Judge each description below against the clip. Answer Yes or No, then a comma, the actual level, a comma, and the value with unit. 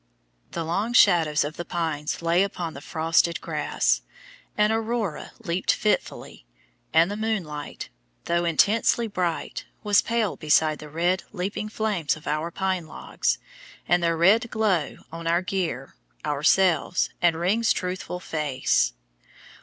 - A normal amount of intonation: Yes, average, 4.1 semitones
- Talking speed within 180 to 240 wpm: No, slow, 135 wpm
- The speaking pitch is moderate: Yes, medium, 175 Hz